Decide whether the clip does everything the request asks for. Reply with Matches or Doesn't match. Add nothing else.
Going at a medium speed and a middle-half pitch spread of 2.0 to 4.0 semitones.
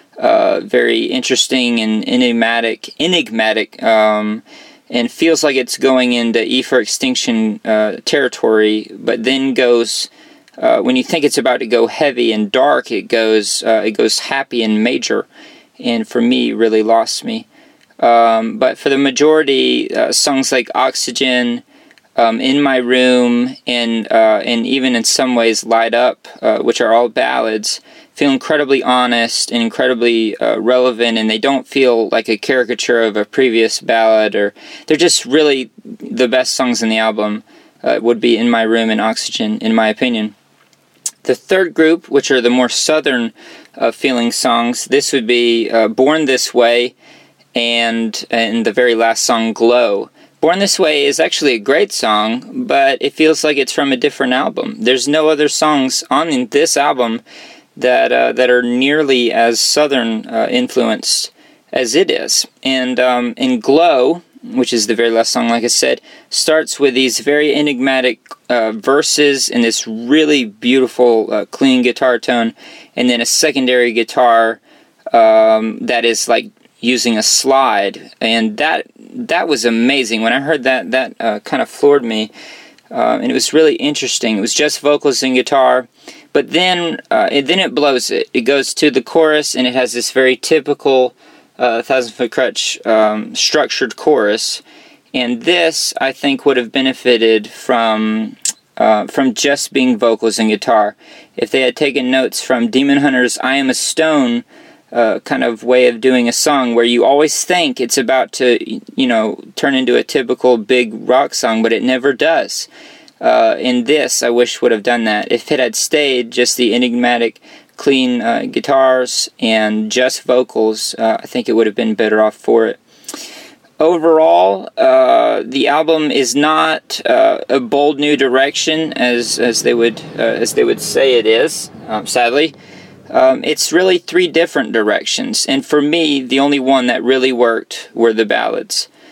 Doesn't match